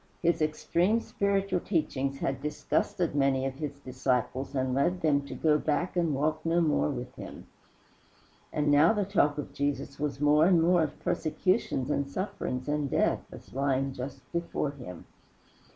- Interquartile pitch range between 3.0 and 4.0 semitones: Yes, average, 3.7 semitones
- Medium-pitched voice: Yes, medium, 150 Hz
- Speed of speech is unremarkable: Yes, average, 165 wpm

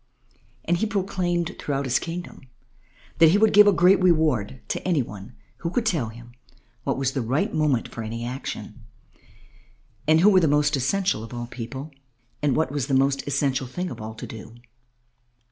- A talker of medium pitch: Yes, medium, 145 Hz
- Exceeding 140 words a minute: Yes, average, 185 wpm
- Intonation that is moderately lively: No, wide, 6.0 semitones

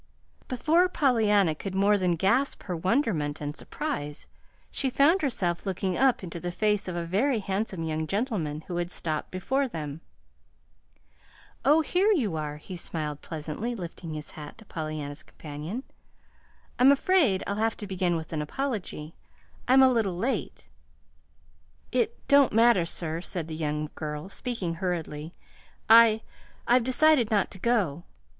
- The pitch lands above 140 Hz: Yes, high, 190 Hz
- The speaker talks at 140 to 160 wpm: Yes, average, 150 wpm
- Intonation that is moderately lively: No, wide, 7.2 semitones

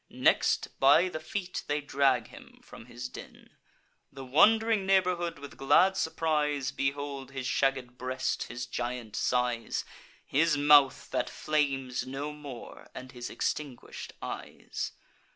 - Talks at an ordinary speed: No, slow, 130 wpm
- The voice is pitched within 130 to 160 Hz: Yes, medium, 140 Hz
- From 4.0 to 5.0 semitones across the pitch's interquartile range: No, average, 3.2 semitones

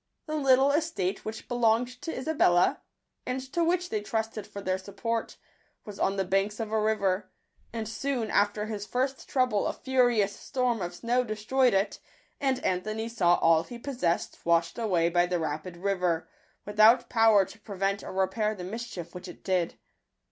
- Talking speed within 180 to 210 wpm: No, average, 170 wpm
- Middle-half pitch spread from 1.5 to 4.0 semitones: No, average, 4.5 semitones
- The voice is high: Yes, high, 215 Hz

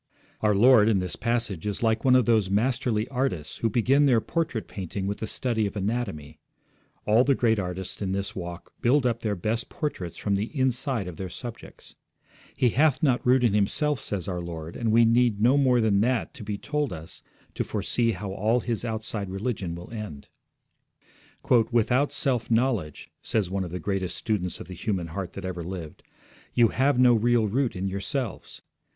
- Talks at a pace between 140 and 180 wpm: No, average, 190 wpm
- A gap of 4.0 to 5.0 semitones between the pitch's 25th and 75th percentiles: Yes, average, 4.3 semitones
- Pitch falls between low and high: No, low, 110 Hz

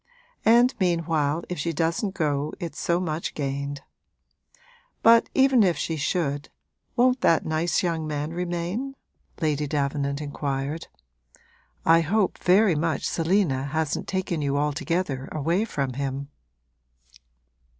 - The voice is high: No, medium, 160 Hz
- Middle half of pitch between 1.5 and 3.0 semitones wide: No, average, 3.8 semitones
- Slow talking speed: Yes, slow, 120 wpm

